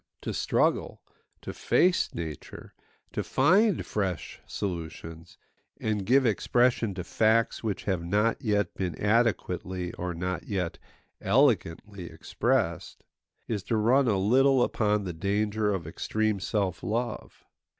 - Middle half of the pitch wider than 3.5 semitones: Yes, average, 4.0 semitones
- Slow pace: Yes, slow, 125 wpm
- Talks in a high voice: No, low, 105 Hz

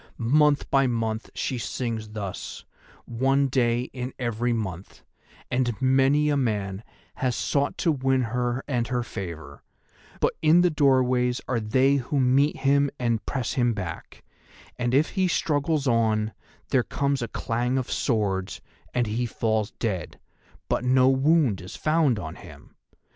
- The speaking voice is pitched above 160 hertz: No, low, 125 Hz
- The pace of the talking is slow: No, average, 155 wpm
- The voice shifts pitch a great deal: No, average, 3.4 semitones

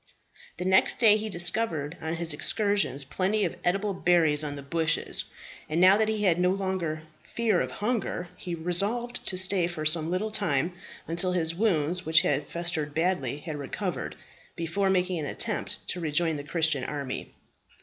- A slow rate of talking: No, average, 170 wpm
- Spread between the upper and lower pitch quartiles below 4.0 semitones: Yes, average, 3.6 semitones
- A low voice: No, medium, 175 Hz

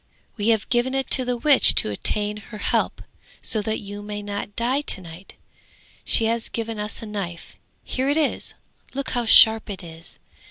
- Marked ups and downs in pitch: No, average, 2.9 semitones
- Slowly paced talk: No, average, 195 wpm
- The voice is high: Yes, high, 220 Hz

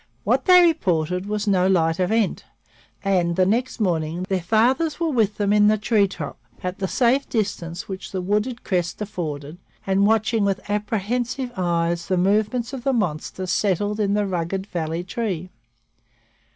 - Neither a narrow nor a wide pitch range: Yes, average, 3.6 semitones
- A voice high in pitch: Yes, high, 200 Hz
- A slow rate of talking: No, average, 160 wpm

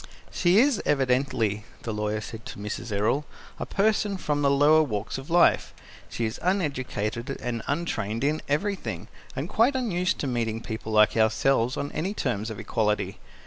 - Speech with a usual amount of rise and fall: No, wide, 7.3 semitones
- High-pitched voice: No, low, 130 Hz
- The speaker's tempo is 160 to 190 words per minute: Yes, average, 165 wpm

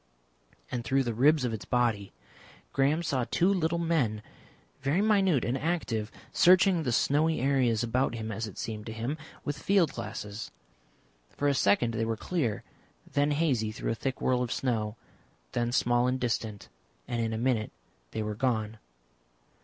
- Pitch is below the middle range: Yes, low, 125 Hz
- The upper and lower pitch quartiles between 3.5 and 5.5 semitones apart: Yes, average, 4.5 semitones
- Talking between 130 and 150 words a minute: No, average, 170 wpm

